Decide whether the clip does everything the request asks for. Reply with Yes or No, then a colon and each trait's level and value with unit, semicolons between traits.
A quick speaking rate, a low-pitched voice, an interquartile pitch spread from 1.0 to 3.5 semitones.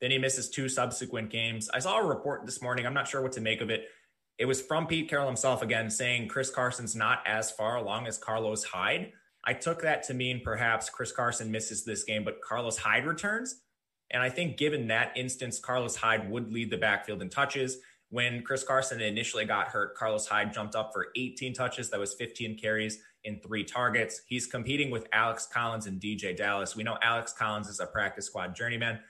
Yes: fast, 210 wpm; low, 120 Hz; average, 2.8 semitones